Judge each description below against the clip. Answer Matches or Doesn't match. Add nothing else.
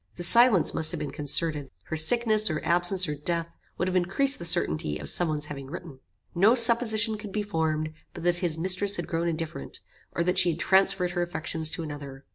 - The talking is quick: Matches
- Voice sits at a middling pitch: Matches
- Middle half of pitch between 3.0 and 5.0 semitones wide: Matches